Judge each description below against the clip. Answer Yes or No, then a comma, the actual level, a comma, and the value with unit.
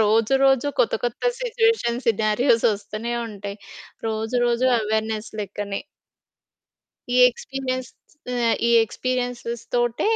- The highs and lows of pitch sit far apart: No, average, 2.8 semitones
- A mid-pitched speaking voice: No, high, 235 Hz